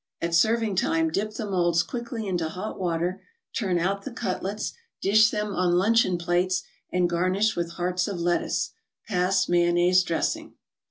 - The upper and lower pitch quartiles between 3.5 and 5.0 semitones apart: No, average, 2.7 semitones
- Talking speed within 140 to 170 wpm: Yes, average, 155 wpm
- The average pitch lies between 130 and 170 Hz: No, medium, 185 Hz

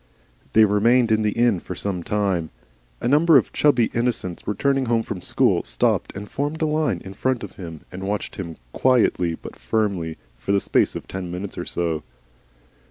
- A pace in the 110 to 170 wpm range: No, average, 185 wpm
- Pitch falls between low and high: No, low, 105 Hz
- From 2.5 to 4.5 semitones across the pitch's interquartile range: No, average, 5.0 semitones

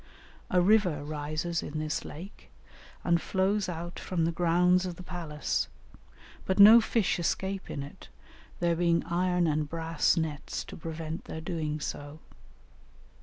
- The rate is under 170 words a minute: Yes, average, 145 wpm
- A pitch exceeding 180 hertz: No, medium, 170 Hz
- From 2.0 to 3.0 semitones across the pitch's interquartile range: Yes, narrow, 2.6 semitones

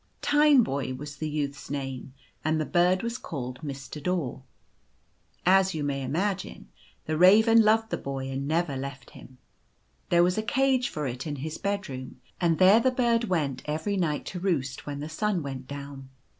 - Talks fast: No, average, 175 wpm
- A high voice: No, medium, 155 Hz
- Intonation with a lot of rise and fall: Yes, wide, 6.0 semitones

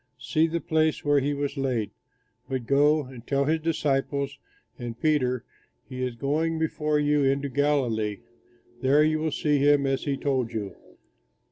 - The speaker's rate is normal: Yes, average, 160 wpm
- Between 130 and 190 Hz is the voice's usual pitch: Yes, medium, 140 Hz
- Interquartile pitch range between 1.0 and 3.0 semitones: Yes, average, 2.7 semitones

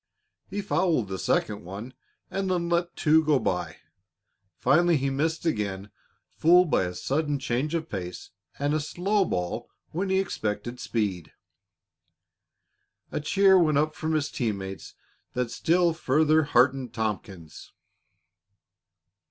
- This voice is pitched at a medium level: Yes, medium, 145 Hz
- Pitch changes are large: Yes, wide, 7.8 semitones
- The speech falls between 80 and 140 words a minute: Yes, slow, 135 wpm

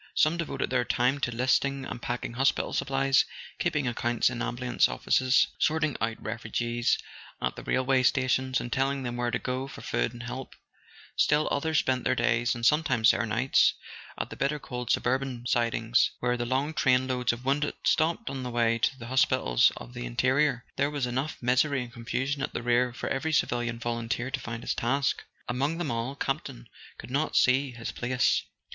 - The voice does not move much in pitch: Yes, narrow, 2.3 semitones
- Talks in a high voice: No, low, 125 Hz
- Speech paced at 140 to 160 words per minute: No, average, 190 wpm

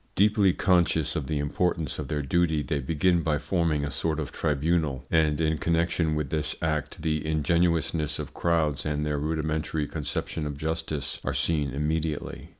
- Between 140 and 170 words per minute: Yes, average, 165 wpm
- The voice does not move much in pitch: Yes, narrow, 1.9 semitones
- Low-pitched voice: Yes, very low, 80 Hz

